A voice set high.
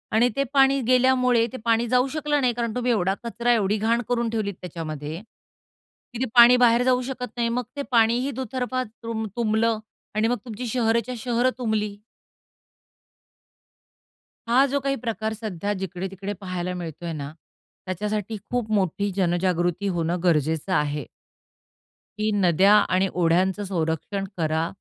Yes: high, 220 Hz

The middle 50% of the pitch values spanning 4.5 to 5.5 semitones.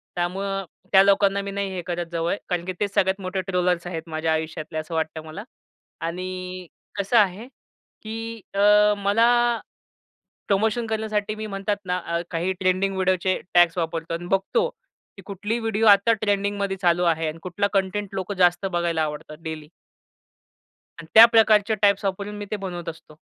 No: average, 2.9 semitones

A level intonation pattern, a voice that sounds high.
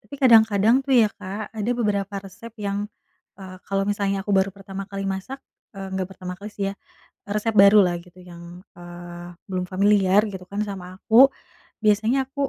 Yes: narrow, 2.0 semitones; high, 200 Hz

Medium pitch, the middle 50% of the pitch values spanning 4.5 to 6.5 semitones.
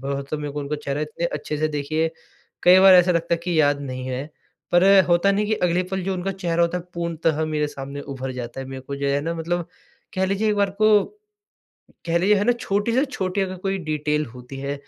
Yes: medium, 165 Hz; average, 4.8 semitones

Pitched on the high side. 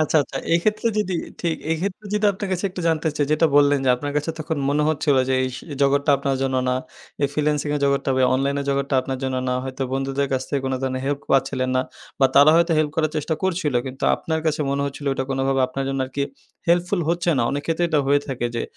No: medium, 140 Hz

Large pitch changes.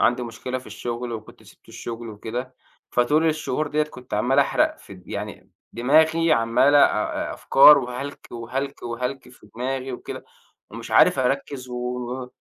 No: average, 2.8 semitones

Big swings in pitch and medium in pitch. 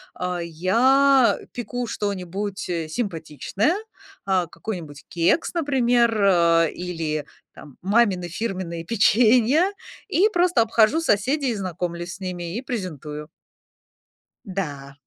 No: wide, 5.9 semitones; high, 195 Hz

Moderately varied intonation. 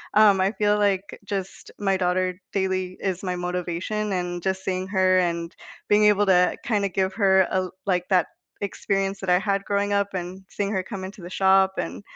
No: narrow, 1.7 semitones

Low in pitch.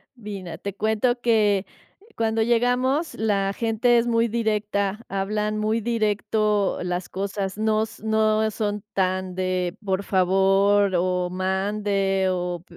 No: high, 205 Hz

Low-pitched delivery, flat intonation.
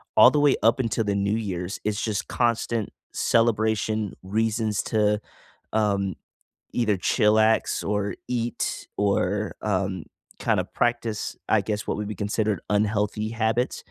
Yes: low, 105 Hz; narrow, 1.6 semitones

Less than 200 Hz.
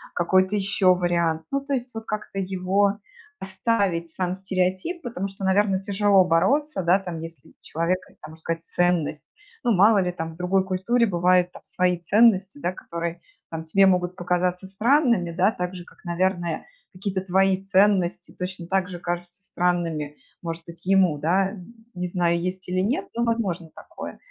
Yes: medium, 185 Hz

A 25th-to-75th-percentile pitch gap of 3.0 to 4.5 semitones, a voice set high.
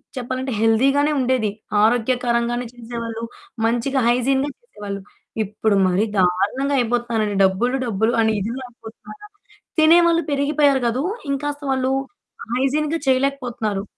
Yes: average, 3.5 semitones; high, 245 Hz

